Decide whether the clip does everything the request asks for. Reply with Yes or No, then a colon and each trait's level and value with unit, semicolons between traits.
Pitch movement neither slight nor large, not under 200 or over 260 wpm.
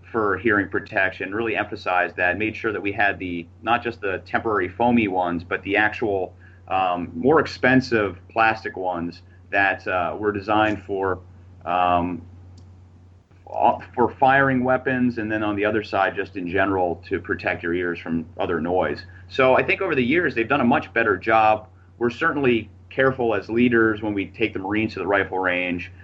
No: average, 3.6 semitones; average, 175 wpm